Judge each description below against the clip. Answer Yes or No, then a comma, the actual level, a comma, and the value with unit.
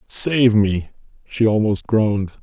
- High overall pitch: No, low, 110 Hz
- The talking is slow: Yes, slow, 125 wpm